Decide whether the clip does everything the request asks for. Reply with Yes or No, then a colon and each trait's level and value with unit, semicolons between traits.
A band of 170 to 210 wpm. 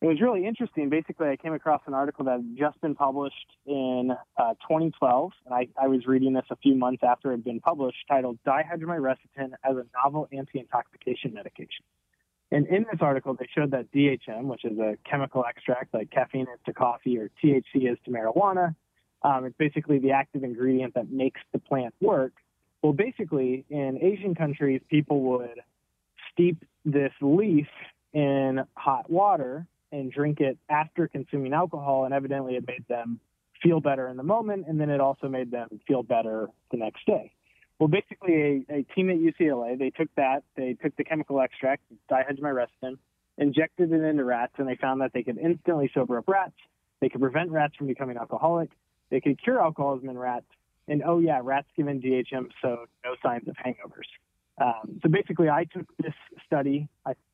Yes: average, 185 wpm